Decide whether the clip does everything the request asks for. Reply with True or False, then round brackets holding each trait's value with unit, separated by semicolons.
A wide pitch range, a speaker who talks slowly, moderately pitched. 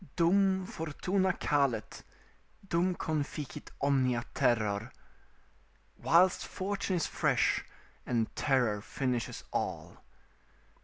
True (6.9 semitones; 85 wpm; 145 Hz)